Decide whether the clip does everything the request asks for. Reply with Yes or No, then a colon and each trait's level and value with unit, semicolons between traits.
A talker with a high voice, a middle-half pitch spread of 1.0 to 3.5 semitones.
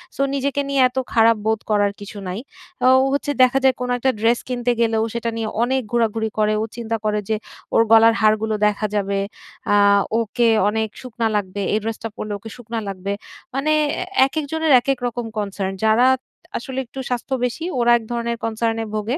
Yes: high, 230 Hz; narrow, 2.5 semitones